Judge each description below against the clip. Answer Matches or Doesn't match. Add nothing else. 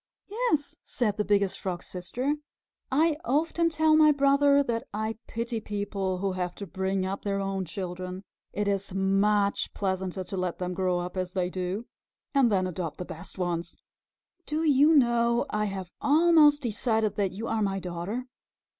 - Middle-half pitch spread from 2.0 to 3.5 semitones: Doesn't match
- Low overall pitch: Doesn't match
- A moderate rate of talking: Matches